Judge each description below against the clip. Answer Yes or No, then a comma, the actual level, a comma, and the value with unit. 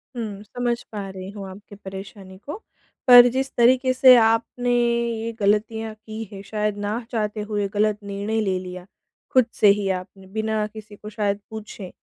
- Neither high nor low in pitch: No, high, 215 Hz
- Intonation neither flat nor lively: No, narrow, 2.3 semitones